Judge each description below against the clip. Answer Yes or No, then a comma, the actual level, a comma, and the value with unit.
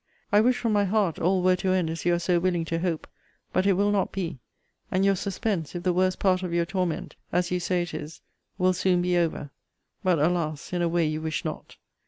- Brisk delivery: Yes, fast, 240 wpm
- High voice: No, medium, 180 Hz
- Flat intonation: Yes, narrow, 1.9 semitones